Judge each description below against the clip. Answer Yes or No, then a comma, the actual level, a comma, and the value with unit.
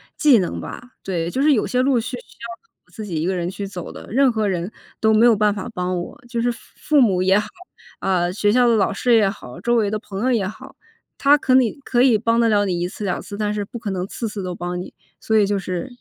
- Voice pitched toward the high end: Yes, high, 210 Hz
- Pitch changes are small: No, average, 4.1 semitones